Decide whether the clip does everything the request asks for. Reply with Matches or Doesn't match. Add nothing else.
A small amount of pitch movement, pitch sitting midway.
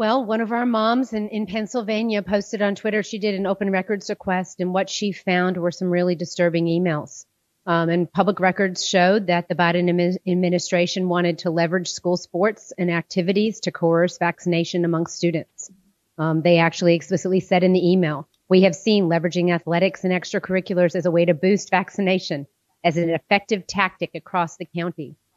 Matches